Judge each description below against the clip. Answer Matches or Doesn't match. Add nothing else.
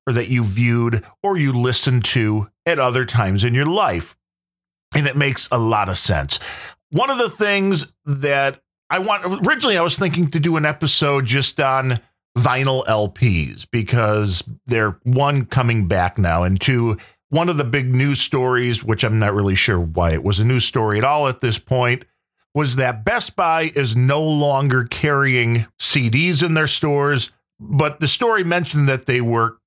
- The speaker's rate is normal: Matches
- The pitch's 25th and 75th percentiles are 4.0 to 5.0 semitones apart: Matches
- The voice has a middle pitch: Doesn't match